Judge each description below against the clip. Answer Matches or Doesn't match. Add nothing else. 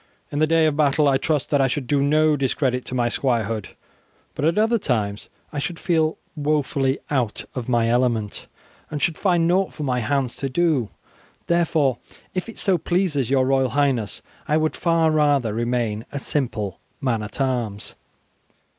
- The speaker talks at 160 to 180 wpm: Matches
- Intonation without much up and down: Doesn't match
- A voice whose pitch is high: Doesn't match